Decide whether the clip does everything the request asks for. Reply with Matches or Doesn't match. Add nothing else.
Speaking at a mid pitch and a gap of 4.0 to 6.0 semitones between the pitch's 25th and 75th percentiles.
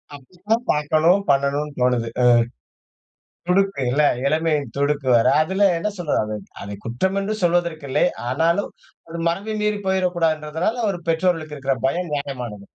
Matches